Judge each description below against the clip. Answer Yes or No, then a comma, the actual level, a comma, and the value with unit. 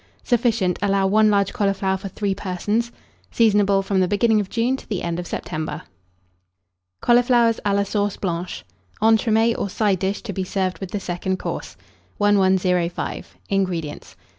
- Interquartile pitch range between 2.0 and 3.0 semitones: Yes, narrow, 2.6 semitones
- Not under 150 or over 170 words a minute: Yes, average, 155 wpm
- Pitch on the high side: Yes, high, 200 Hz